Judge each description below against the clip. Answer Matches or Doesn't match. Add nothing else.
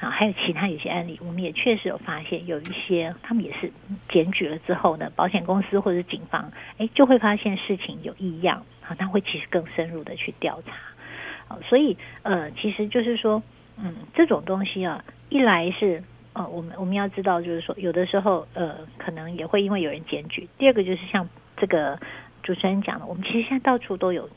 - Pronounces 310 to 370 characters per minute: Matches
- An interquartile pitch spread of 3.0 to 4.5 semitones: Matches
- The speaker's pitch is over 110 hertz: Matches